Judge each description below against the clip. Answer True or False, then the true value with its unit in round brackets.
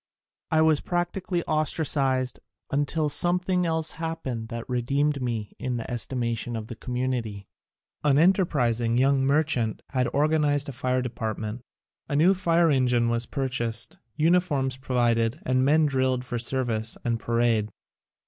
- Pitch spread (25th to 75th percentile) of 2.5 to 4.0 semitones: False (4.6 semitones)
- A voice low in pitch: True (130 Hz)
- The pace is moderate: True (150 wpm)